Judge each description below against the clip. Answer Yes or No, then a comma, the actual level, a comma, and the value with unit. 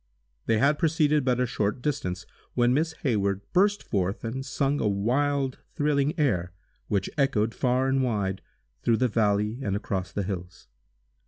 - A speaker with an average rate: Yes, average, 160 wpm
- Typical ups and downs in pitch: No, wide, 5.7 semitones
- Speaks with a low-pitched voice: Yes, low, 120 Hz